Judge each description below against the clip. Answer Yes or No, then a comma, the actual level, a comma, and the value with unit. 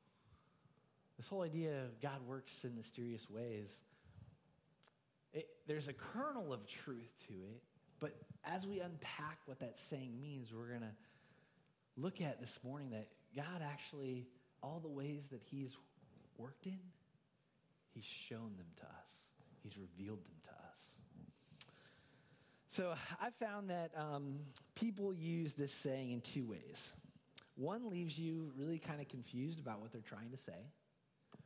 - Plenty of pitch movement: No, average, 4.8 semitones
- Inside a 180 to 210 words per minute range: No, average, 145 wpm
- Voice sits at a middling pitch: Yes, medium, 145 Hz